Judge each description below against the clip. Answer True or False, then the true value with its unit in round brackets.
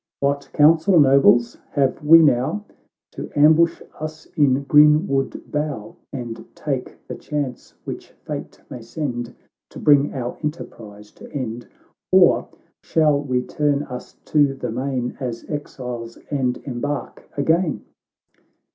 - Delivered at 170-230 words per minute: False (135 wpm)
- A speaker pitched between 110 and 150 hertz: True (140 Hz)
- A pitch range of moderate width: True (3.3 semitones)